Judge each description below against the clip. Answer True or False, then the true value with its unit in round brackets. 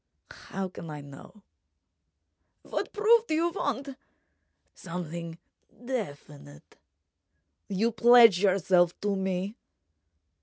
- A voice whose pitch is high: True (195 Hz)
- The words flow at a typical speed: False (90 wpm)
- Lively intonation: True (6.0 semitones)